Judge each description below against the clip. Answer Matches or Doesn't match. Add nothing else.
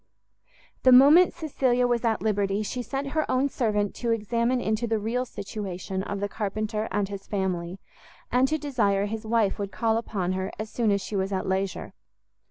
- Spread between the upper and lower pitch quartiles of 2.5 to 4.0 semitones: Matches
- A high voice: Matches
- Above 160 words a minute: Matches